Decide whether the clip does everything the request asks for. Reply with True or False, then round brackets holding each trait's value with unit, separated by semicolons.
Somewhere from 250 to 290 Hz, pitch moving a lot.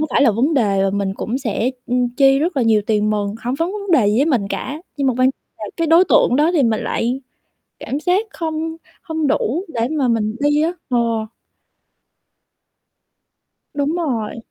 True (260 Hz; 5.7 semitones)